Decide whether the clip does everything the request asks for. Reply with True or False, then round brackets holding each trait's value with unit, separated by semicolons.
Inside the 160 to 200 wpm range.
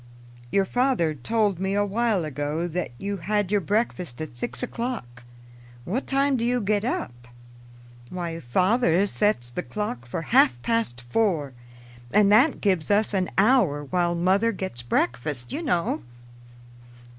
False (145 wpm)